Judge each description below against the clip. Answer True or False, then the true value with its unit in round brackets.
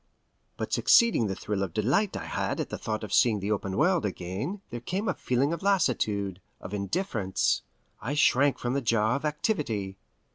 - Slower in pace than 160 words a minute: False (180 wpm)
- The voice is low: True (120 Hz)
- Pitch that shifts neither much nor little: False (7.1 semitones)